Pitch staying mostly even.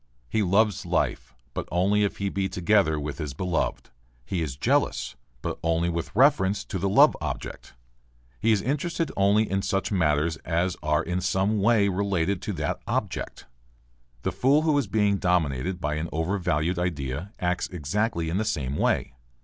No: average, 3.9 semitones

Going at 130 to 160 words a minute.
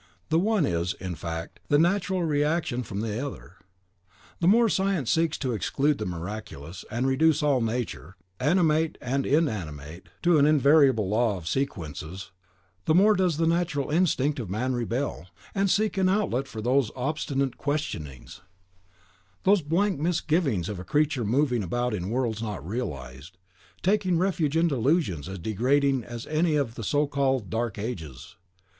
Yes: average, 155 wpm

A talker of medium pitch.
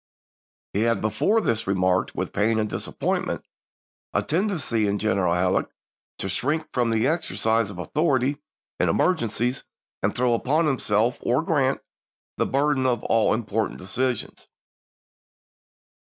No: low, 115 Hz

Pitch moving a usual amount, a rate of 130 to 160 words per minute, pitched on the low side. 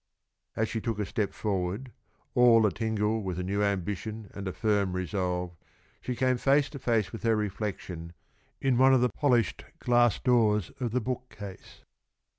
No: average, 3.7 semitones; average, 170 wpm; low, 110 Hz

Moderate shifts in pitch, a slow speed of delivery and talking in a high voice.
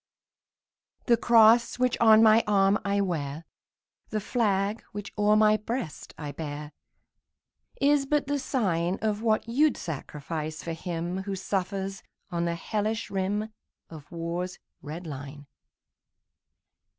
Yes: average, 4.7 semitones; slow, 130 wpm; high, 195 Hz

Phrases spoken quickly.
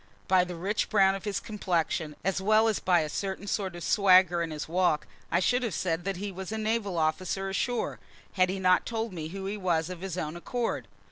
Yes: fast, 225 wpm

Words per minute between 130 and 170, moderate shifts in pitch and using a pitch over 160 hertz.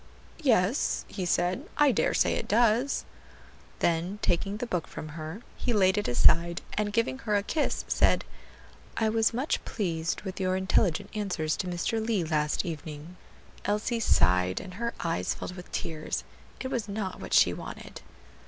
Yes: average, 165 wpm; average, 4.7 semitones; high, 190 Hz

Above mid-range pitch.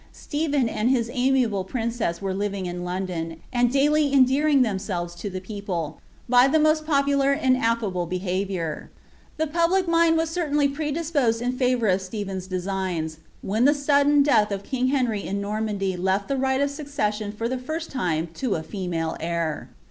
Yes: high, 230 Hz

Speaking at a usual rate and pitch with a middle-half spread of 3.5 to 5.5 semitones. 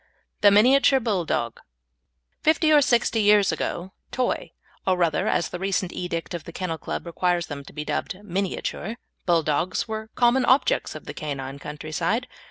Yes: average, 165 wpm; average, 5.1 semitones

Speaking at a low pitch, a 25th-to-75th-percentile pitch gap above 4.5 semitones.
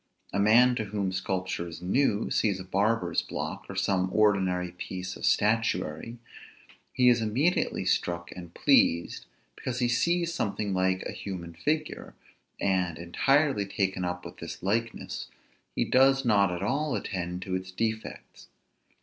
No: low, 100 Hz; average, 4.2 semitones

